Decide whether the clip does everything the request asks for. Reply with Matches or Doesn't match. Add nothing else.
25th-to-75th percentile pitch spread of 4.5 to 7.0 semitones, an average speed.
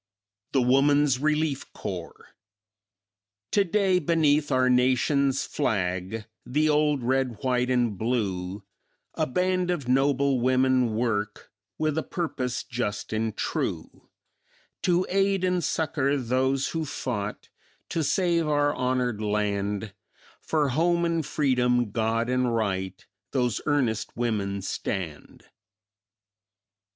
Doesn't match